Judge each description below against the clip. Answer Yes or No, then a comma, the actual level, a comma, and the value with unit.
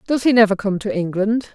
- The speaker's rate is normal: No, fast, 235 wpm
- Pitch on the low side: No, high, 210 Hz